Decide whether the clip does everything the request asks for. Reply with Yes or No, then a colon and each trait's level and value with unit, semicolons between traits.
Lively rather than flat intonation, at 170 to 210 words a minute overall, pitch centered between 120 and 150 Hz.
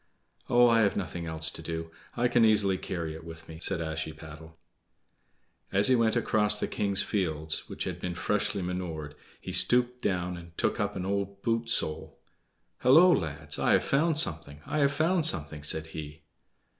No: wide, 6.2 semitones; average, 180 wpm; very low, 90 Hz